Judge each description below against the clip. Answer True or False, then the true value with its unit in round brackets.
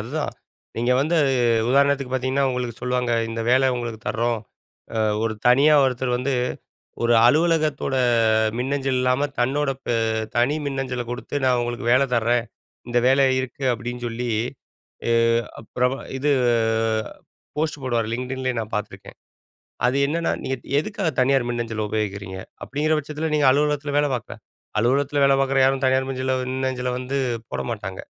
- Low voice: True (130 Hz)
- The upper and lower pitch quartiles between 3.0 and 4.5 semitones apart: False (2.5 semitones)